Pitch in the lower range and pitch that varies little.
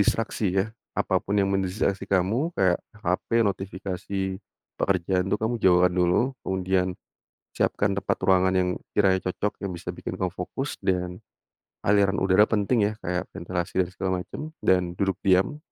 Yes: very low, 95 Hz; narrow, 1.5 semitones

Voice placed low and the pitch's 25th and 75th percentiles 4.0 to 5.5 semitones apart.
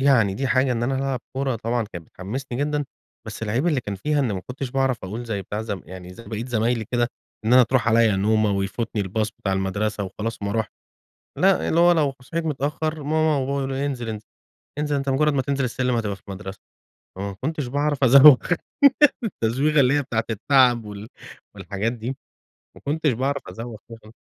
Yes: low, 120 Hz; average, 4.5 semitones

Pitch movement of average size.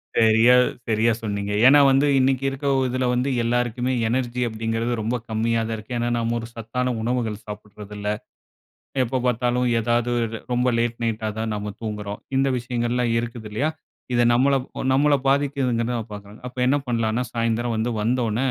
No: narrow, 2.0 semitones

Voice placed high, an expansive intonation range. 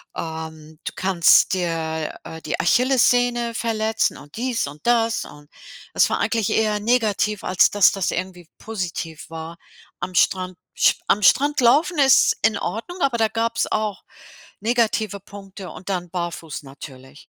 Yes: high, 200 Hz; wide, 5.7 semitones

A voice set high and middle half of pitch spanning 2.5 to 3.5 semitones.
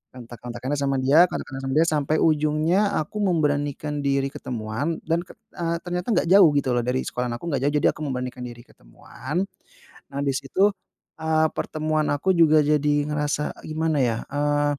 No: medium, 145 Hz; average, 2.9 semitones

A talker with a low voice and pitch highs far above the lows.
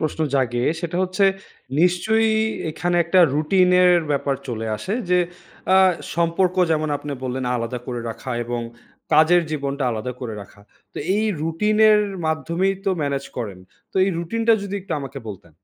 No: medium, 160 Hz; wide, 6.2 semitones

